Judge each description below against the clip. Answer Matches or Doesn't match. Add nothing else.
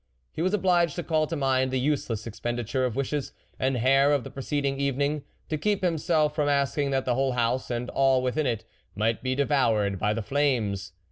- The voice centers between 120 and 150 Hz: Matches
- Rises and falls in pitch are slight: Doesn't match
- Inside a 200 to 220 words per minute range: Matches